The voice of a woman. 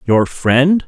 No: male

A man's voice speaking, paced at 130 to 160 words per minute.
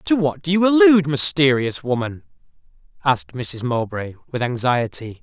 Yes: male; average, 140 wpm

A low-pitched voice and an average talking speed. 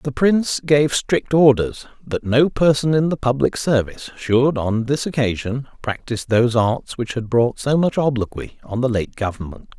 Yes: low, 125 Hz; average, 180 wpm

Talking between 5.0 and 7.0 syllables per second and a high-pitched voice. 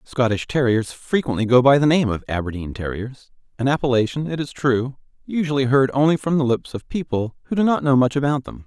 No: 5.7 syllables/s; low, 130 Hz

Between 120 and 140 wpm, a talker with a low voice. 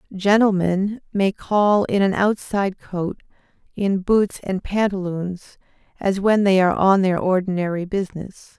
No: slow, 135 wpm; high, 195 Hz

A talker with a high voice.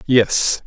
No: low, 120 Hz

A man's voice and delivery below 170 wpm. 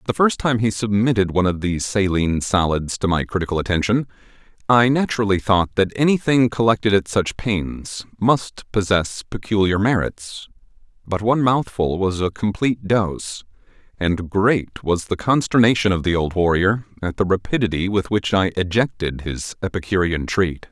Yes: male; average, 155 wpm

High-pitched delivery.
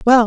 Yes: high, 235 Hz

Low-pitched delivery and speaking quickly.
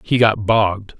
No: low, 105 Hz; average, 180 wpm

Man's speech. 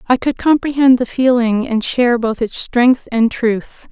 No: female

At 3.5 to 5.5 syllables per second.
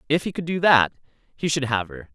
No: 5.8 syllables/s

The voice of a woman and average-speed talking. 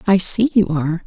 No: female; fast, 225 wpm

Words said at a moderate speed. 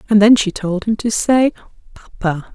Yes: average, 190 wpm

